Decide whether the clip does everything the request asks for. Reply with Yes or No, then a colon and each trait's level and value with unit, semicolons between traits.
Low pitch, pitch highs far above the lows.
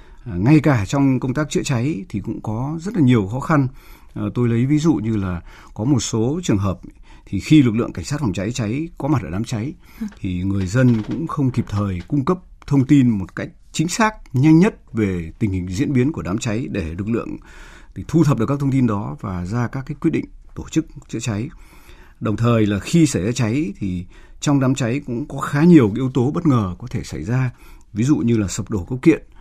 Yes: low, 120 Hz; wide, 5.8 semitones